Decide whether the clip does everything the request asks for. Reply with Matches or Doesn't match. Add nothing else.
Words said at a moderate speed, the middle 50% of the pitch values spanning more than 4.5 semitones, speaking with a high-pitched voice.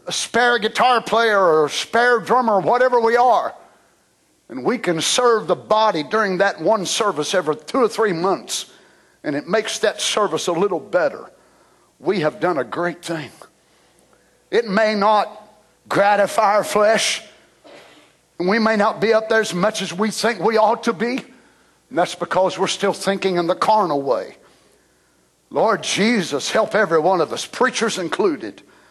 Doesn't match